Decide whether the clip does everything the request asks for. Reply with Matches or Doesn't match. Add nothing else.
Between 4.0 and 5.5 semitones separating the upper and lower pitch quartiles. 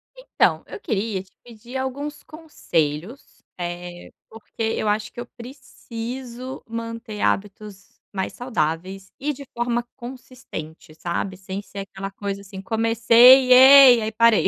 Matches